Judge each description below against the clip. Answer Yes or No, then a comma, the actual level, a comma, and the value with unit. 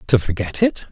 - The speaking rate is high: No, average, 195 wpm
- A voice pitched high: No, low, 120 Hz